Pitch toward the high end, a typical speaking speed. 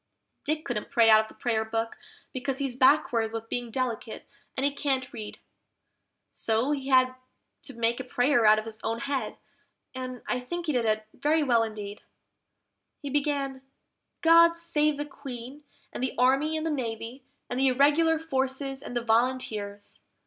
Yes: very high, 255 Hz; average, 170 wpm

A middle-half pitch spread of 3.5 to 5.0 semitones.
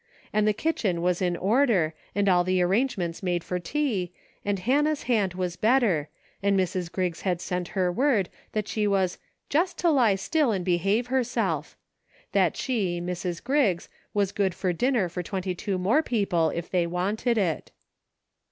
Yes: average, 4.6 semitones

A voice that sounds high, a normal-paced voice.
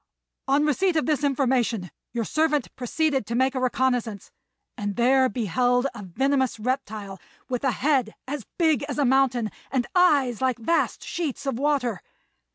Yes: very high, 260 Hz; average, 160 wpm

